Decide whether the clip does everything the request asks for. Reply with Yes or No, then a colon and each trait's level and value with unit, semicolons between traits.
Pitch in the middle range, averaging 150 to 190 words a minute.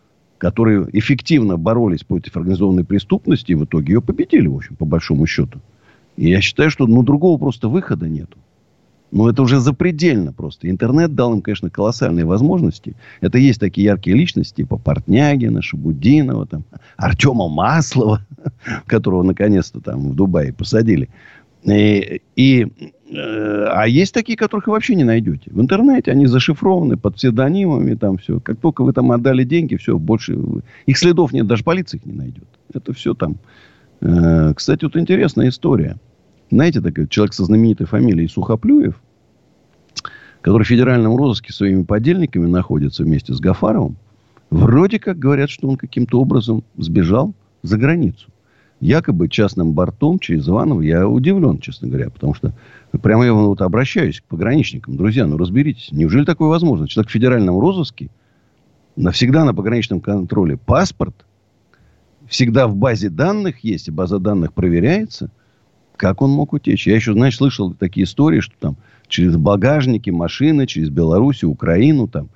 No: low, 115 Hz; average, 155 wpm